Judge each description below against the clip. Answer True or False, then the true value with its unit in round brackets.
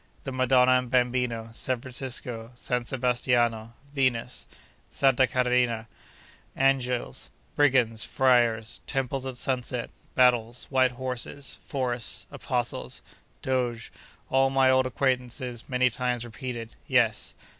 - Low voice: True (125 Hz)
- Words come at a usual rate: False (100 wpm)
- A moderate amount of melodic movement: False (1.5 semitones)